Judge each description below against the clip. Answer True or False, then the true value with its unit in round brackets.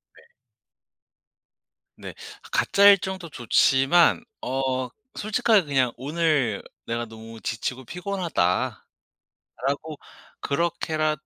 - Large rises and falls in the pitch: True (5.8 semitones)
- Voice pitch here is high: False (145 Hz)